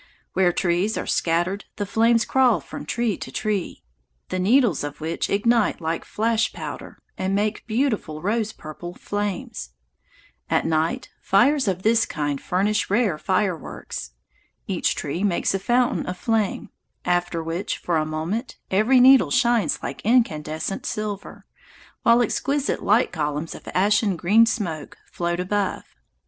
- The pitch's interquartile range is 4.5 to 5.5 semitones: Yes, average, 4.8 semitones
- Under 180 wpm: Yes, average, 140 wpm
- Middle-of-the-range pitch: No, high, 200 Hz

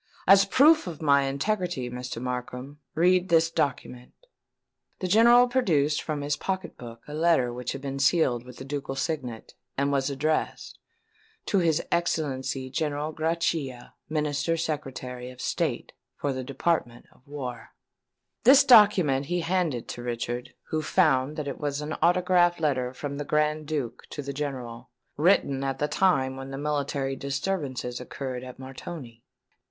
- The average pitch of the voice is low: No, medium, 145 Hz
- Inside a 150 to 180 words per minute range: Yes, average, 155 wpm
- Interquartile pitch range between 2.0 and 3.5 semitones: No, average, 4.1 semitones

